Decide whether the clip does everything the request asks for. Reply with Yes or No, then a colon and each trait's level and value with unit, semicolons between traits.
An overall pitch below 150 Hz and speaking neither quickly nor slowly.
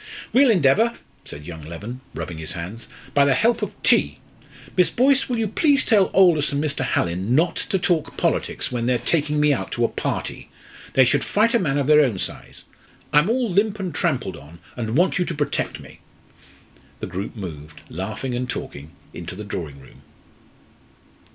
Yes: medium, 140 Hz; average, 185 wpm